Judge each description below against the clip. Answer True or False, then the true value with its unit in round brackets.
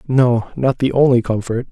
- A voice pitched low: True (125 Hz)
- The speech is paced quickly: False (175 wpm)